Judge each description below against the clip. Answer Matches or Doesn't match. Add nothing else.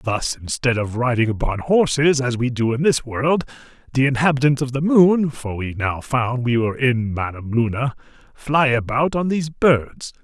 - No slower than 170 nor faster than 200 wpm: Matches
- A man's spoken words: Matches